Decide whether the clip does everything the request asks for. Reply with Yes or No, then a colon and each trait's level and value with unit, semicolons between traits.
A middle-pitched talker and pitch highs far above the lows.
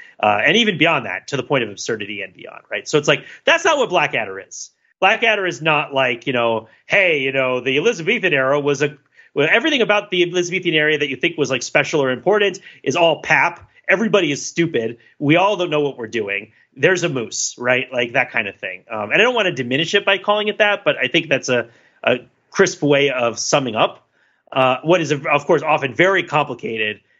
Yes: medium, 150 Hz; wide, 6.5 semitones